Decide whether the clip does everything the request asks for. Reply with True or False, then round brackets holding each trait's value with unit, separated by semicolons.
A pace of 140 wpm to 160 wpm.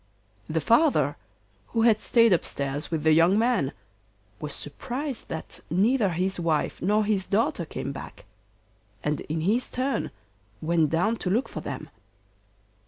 True (145 wpm)